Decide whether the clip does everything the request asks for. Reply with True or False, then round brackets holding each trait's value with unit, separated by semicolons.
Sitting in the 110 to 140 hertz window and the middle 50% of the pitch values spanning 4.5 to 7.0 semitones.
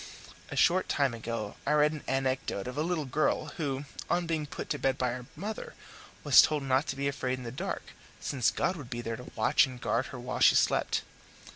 False (135 Hz; 3.2 semitones)